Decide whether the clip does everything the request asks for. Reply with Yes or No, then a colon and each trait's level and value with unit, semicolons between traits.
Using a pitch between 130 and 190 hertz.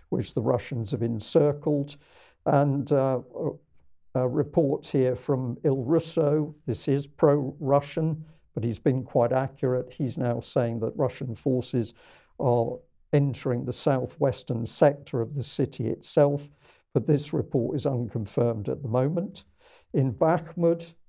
Yes: medium, 140 Hz